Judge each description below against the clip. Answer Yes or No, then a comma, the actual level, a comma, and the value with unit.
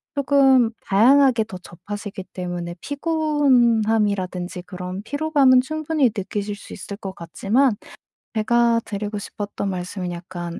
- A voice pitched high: Yes, high, 210 Hz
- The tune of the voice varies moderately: No, wide, 5.9 semitones